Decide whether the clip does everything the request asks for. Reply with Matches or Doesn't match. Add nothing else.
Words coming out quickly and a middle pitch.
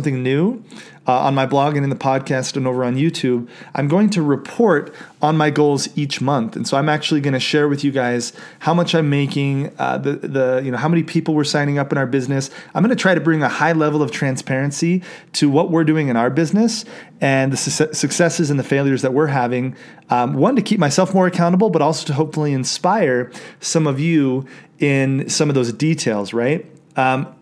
Matches